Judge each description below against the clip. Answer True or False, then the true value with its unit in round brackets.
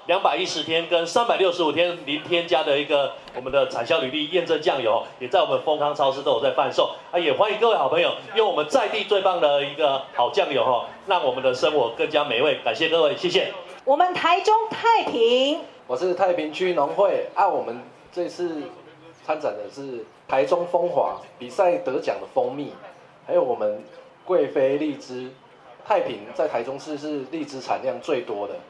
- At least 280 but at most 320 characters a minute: True (285 characters per minute)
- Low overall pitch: False (175 Hz)